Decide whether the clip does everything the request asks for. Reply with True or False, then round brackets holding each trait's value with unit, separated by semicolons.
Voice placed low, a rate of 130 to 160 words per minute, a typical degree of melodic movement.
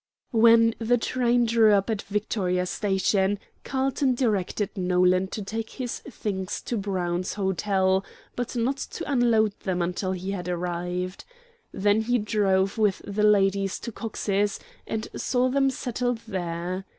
False (205 Hz; 140 wpm; 3.5 semitones)